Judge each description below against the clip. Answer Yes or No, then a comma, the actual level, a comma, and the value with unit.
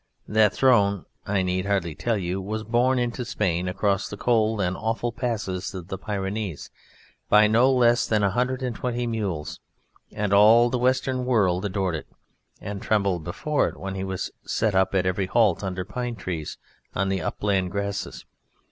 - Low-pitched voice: Yes, low, 100 Hz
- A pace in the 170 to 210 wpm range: Yes, average, 175 wpm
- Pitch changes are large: No, average, 3.8 semitones